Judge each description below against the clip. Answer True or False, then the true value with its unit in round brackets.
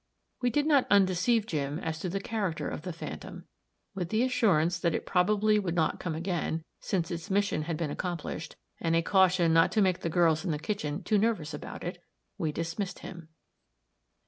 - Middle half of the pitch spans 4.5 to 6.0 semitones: False (3.7 semitones)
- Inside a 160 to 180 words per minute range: False (195 wpm)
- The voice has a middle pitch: True (175 Hz)